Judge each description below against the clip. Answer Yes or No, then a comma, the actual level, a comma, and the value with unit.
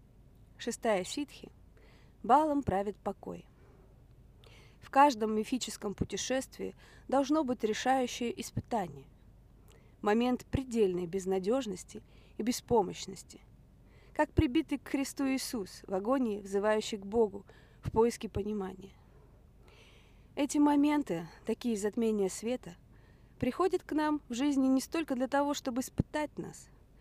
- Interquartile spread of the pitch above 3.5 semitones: Yes, wide, 5.5 semitones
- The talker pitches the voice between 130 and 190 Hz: No, high, 235 Hz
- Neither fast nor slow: No, slow, 105 wpm